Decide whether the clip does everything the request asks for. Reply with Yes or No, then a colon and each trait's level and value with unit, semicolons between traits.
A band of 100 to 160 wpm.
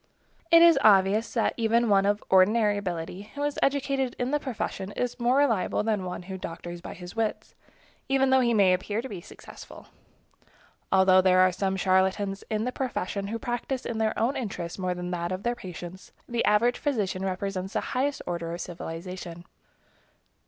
No: average, 185 wpm